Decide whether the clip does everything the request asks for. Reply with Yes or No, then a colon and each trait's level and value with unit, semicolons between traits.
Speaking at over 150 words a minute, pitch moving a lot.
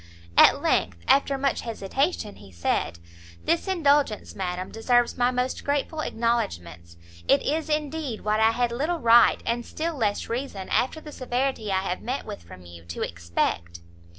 Yes: average, 160 wpm; wide, 7.2 semitones